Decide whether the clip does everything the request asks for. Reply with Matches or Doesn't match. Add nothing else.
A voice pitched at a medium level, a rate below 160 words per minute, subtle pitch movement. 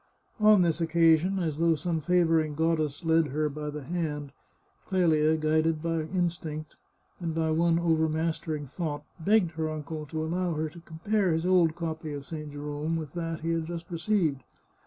Doesn't match